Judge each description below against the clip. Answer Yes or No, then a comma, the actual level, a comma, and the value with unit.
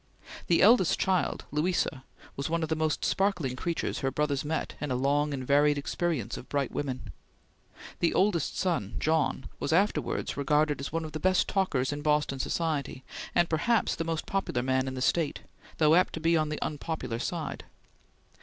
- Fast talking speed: No, average, 180 wpm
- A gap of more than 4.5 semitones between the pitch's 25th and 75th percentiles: No, average, 3.3 semitones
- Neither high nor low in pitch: Yes, medium, 150 Hz